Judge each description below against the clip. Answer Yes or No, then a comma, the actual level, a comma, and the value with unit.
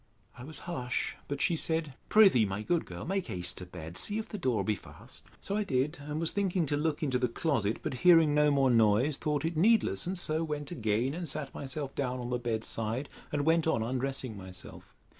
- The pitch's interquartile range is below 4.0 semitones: No, average, 5.3 semitones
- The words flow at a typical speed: No, fast, 220 wpm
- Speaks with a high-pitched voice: No, medium, 140 Hz